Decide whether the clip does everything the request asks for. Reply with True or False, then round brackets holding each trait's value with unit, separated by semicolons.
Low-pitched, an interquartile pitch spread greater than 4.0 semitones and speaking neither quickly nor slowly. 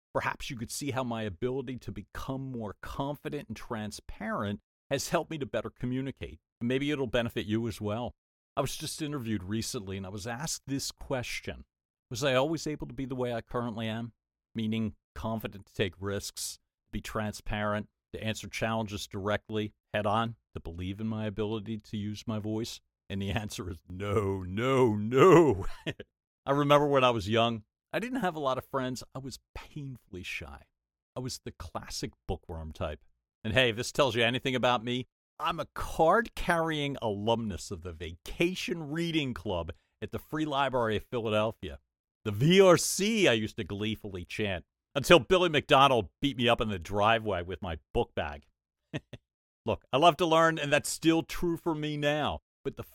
True (115 Hz; 4.7 semitones; 180 wpm)